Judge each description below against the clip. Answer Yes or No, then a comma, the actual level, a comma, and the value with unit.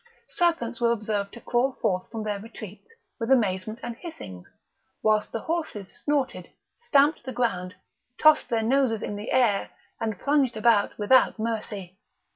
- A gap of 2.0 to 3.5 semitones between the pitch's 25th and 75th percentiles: No, average, 4.0 semitones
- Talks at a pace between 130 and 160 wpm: Yes, average, 150 wpm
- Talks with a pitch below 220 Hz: No, high, 230 Hz